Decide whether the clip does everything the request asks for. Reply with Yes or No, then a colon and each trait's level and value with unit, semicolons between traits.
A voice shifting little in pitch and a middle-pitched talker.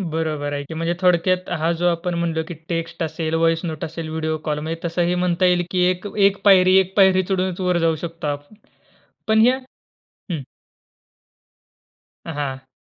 Yes: narrow, 2.3 semitones; medium, 170 Hz